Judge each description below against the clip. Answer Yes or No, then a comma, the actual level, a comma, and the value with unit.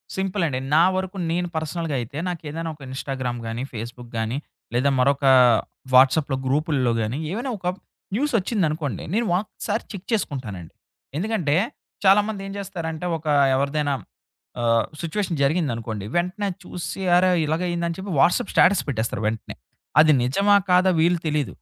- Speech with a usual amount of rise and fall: No, wide, 5.9 semitones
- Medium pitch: Yes, medium, 160 Hz